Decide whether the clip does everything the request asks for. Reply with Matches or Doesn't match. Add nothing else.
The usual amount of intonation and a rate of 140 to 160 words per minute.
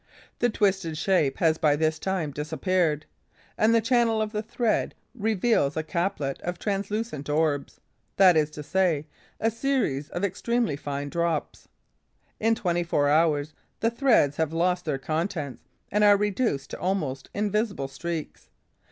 Doesn't match